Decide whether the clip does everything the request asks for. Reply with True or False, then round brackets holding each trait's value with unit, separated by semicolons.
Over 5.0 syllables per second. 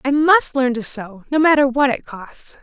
False (4.5 syllables/s)